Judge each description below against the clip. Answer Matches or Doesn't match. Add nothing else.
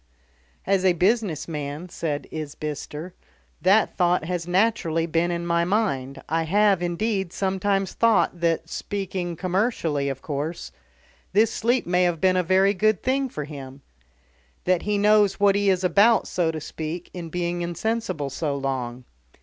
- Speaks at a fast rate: Doesn't match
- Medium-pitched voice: Matches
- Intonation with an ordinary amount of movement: Matches